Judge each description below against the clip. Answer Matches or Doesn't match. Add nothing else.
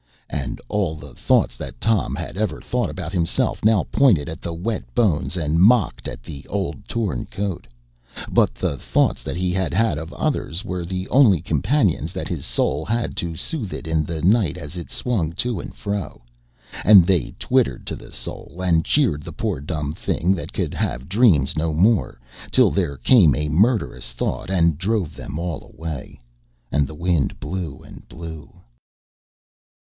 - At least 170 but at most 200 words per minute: Matches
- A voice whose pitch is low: Matches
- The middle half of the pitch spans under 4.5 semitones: Doesn't match